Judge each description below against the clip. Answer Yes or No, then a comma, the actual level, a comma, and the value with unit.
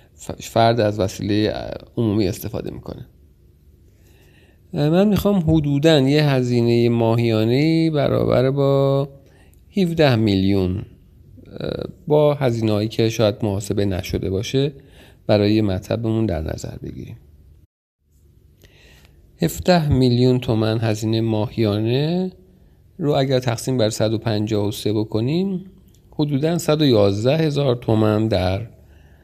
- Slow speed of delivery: Yes, slow, 90 wpm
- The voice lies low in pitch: Yes, low, 110 Hz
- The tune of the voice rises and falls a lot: Yes, wide, 6.0 semitones